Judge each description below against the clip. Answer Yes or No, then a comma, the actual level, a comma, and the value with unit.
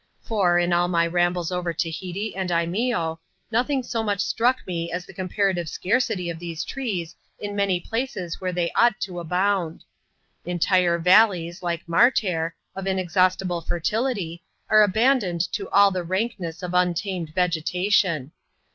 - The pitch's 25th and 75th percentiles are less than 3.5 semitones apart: Yes, average, 3.0 semitones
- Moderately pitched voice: Yes, medium, 180 Hz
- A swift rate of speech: No, average, 145 wpm